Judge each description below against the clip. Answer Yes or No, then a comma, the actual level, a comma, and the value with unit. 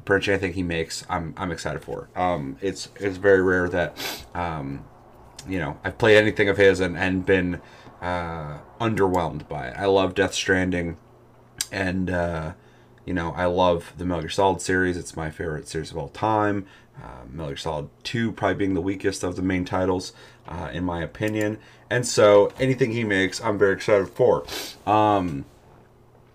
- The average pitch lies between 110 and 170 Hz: No, very low, 95 Hz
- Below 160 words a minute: No, average, 175 wpm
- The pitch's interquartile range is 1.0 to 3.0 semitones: Yes, narrow, 2.4 semitones